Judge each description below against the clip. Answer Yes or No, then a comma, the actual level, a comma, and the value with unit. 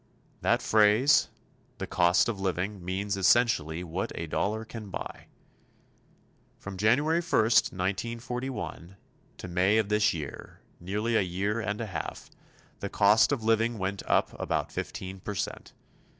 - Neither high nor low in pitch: No, low, 105 Hz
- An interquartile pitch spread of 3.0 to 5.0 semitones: Yes, average, 3.5 semitones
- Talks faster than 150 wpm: No, slow, 135 wpm